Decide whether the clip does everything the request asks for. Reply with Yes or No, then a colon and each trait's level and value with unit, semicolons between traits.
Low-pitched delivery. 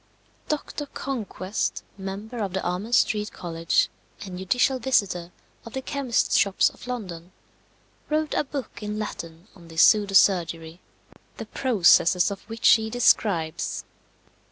No: high, 200 Hz